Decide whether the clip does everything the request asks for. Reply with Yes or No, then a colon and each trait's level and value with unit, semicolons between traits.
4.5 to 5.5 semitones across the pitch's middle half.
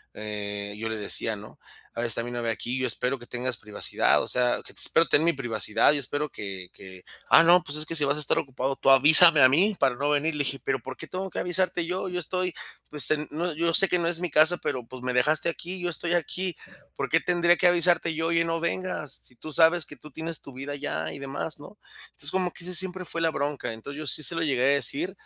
Yes: average, 5.0 semitones